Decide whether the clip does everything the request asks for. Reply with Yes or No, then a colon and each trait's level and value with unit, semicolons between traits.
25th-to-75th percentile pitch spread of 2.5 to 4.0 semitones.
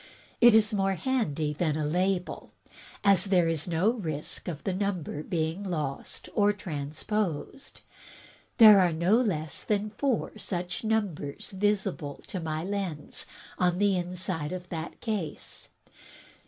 No: average, 4.4 semitones